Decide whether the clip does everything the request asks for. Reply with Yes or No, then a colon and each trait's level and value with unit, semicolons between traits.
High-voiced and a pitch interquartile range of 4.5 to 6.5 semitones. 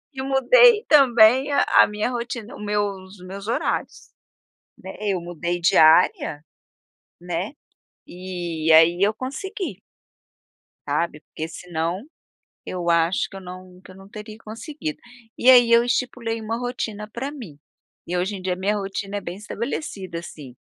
Yes: high, 200 Hz; average, 5.1 semitones